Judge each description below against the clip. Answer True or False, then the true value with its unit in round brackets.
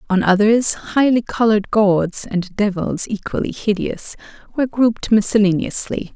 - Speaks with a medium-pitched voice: False (210 Hz)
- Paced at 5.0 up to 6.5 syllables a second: False (4.8 syllables/s)